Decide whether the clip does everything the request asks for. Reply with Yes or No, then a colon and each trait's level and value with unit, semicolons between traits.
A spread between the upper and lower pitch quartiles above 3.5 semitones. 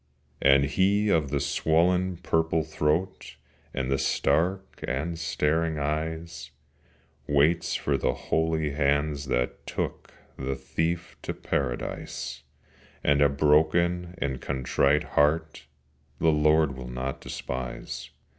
No: average, 2.9 semitones